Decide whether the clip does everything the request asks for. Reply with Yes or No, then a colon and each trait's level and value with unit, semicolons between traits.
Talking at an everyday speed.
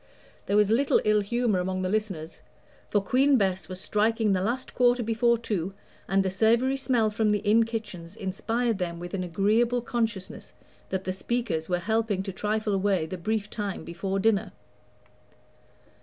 Yes: average, 170 wpm